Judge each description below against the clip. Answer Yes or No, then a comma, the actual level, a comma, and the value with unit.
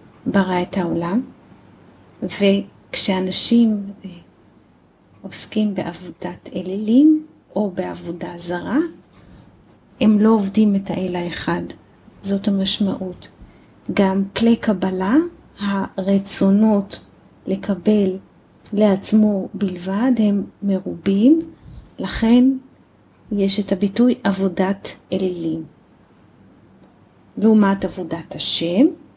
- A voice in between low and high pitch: No, high, 195 Hz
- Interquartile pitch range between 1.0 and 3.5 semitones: Yes, narrow, 2.4 semitones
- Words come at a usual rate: No, slow, 75 wpm